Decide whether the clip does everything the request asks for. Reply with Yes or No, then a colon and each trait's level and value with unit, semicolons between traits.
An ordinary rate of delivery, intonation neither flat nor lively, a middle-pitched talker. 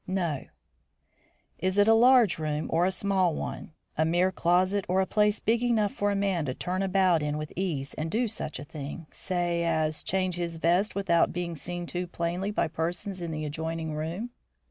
Yes: average, 195 wpm; average, 3.1 semitones; medium, 175 Hz